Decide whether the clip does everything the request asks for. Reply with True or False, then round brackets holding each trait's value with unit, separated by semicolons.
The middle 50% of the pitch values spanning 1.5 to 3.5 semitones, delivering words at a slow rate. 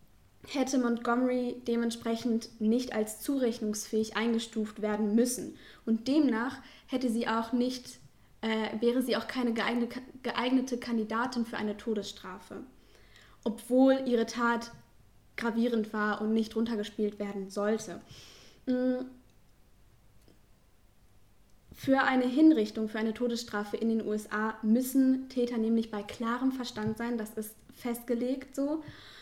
True (2.4 semitones; 115 wpm)